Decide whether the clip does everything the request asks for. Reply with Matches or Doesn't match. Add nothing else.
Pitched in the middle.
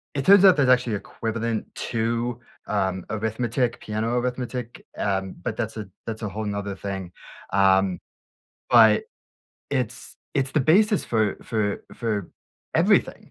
Doesn't match